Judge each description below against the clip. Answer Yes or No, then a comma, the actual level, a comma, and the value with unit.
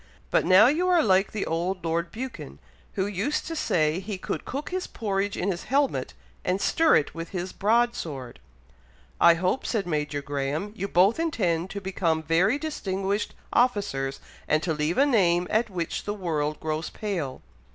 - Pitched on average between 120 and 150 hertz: No, medium, 185 Hz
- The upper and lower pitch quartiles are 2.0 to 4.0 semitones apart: No, average, 4.9 semitones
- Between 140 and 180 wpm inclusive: Yes, average, 175 wpm